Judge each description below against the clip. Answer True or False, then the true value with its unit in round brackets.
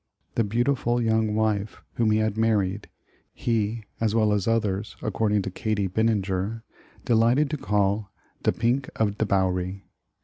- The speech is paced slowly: False (150 wpm)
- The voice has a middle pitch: False (110 Hz)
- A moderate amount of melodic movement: False (2.2 semitones)